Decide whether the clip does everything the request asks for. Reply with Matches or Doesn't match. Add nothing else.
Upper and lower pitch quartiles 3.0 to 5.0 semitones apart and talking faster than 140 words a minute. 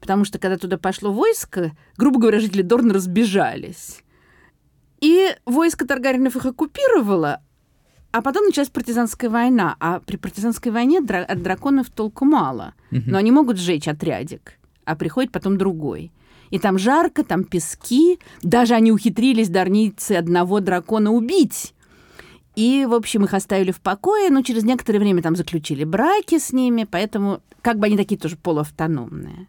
Doesn't match